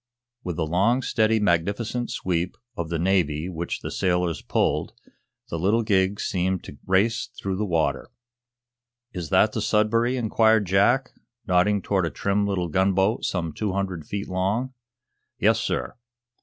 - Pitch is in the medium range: No, very low, 95 Hz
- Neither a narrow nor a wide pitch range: Yes, average, 3.4 semitones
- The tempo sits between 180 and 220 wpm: No, average, 150 wpm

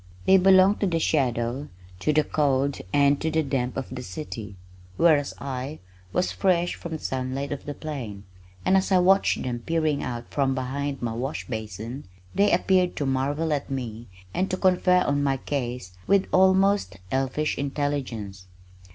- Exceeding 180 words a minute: No, average, 170 wpm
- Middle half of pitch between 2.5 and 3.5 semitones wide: No, average, 4.6 semitones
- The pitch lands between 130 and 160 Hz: Yes, medium, 140 Hz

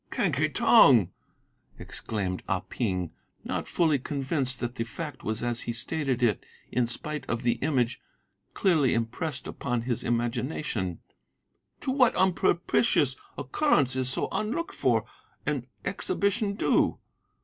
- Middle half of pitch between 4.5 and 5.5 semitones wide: Yes, average, 5.1 semitones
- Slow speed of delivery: Yes, slow, 130 wpm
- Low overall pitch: Yes, low, 130 Hz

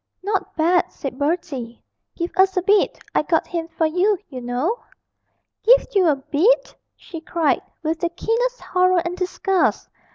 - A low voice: No, very high, 345 Hz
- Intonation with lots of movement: No, average, 3.5 semitones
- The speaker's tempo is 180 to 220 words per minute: No, average, 160 wpm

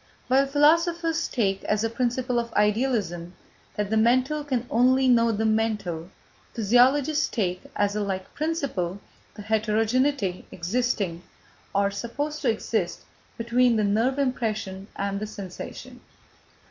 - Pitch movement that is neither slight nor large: Yes, average, 4.2 semitones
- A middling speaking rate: No, slow, 130 wpm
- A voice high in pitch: Yes, high, 225 Hz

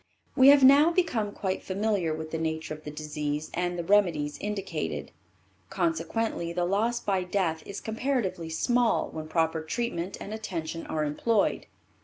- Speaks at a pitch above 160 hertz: Yes, medium, 185 Hz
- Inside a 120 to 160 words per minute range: Yes, average, 155 wpm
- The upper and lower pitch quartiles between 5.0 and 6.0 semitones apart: Yes, wide, 5.5 semitones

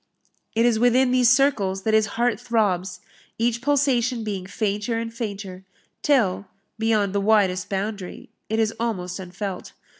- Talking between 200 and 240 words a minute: No, average, 145 wpm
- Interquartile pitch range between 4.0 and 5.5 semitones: No, average, 3.2 semitones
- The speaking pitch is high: Yes, high, 220 Hz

